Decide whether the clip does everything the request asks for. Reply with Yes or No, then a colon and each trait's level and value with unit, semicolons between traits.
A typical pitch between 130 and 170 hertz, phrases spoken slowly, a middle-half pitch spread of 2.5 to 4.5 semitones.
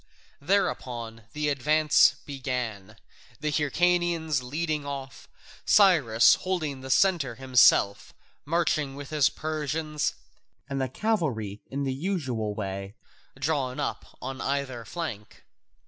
Yes: medium, 140 Hz; slow, 110 wpm; average, 3.9 semitones